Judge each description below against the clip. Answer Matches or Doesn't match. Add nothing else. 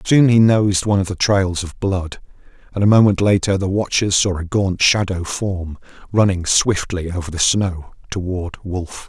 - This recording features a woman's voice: Doesn't match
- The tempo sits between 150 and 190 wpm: Matches